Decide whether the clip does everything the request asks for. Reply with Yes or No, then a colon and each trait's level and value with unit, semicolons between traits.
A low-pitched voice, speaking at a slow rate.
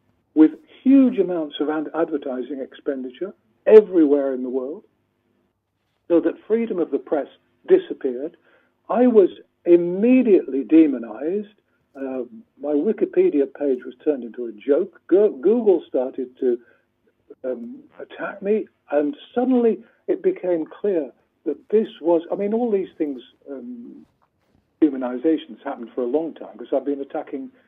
No: medium, 160 Hz; slow, 130 wpm